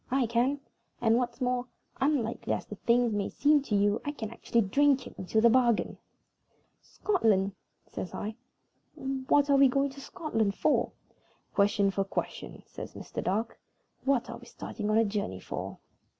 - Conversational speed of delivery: Yes, average, 165 wpm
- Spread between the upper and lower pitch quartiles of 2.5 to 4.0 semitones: No, average, 4.4 semitones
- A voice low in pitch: No, high, 235 Hz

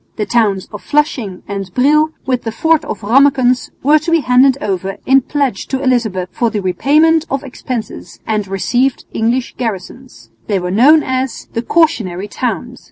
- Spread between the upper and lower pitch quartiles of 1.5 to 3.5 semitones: No, average, 5.0 semitones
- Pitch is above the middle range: Yes, very high, 250 Hz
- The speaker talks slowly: No, average, 165 wpm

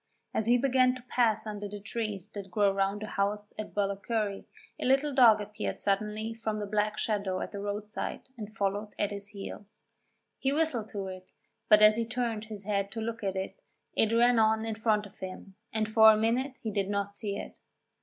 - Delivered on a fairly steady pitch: Yes, narrow, 1.9 semitones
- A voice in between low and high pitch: No, high, 215 Hz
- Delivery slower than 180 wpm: No, fast, 205 wpm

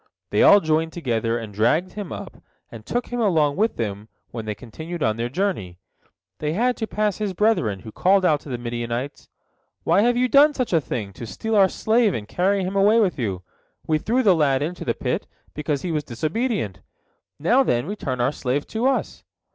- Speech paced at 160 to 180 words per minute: No, fast, 205 wpm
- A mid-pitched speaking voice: Yes, medium, 160 Hz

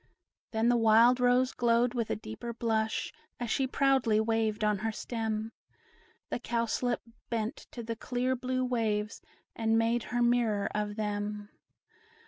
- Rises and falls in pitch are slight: Yes, narrow, 2.0 semitones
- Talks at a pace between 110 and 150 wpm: Yes, average, 145 wpm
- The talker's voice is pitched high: Yes, high, 230 Hz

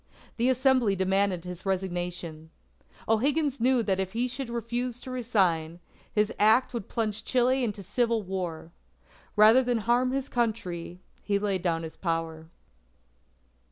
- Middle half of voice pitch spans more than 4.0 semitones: Yes, average, 5.3 semitones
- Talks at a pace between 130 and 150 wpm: Yes, average, 140 wpm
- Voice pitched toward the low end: No, high, 215 Hz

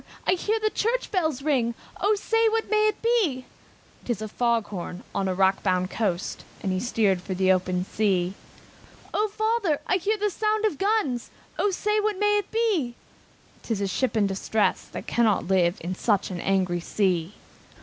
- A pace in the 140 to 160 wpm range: No, average, 180 wpm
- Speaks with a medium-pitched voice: No, high, 240 Hz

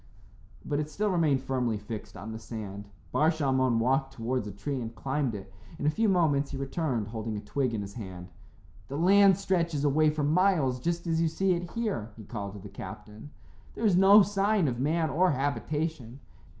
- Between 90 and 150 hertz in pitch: Yes, medium, 140 Hz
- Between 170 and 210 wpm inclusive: Yes, average, 200 wpm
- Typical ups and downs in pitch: No, wide, 6.8 semitones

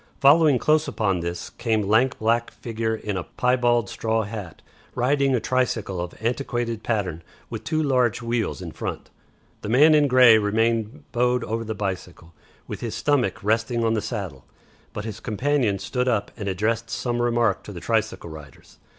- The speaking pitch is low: Yes, low, 115 Hz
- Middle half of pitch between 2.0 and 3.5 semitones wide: Yes, average, 3.2 semitones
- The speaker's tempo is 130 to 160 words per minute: No, average, 170 wpm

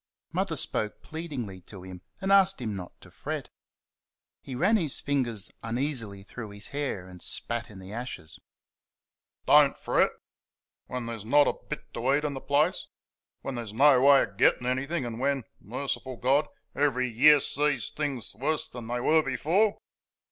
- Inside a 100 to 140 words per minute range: No, average, 165 wpm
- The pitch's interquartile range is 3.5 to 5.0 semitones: Yes, average, 4.5 semitones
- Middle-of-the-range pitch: No, low, 130 Hz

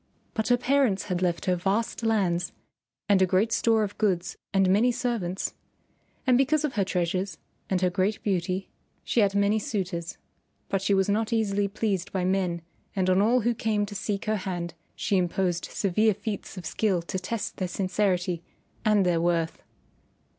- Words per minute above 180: No, average, 175 wpm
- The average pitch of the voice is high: Yes, high, 195 Hz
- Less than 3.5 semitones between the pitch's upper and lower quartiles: Yes, average, 3.0 semitones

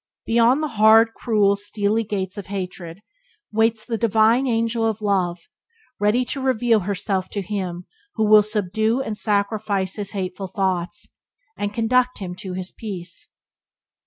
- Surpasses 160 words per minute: No, average, 145 wpm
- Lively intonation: No, average, 2.8 semitones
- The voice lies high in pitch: Yes, high, 210 Hz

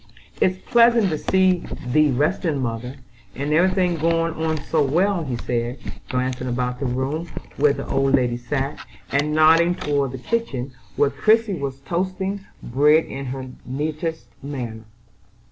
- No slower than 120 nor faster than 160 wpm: Yes, average, 150 wpm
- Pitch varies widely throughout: No, average, 4.6 semitones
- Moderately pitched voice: Yes, medium, 145 Hz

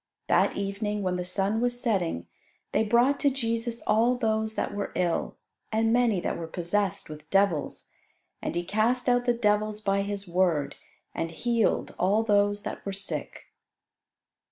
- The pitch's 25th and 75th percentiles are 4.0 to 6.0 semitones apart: No, average, 3.4 semitones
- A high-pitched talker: Yes, high, 205 Hz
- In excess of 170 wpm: No, average, 160 wpm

